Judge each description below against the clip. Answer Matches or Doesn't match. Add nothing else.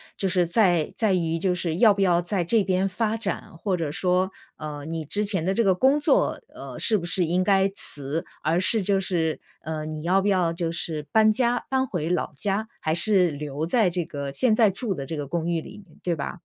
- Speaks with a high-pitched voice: Doesn't match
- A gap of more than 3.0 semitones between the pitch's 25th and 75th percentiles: Matches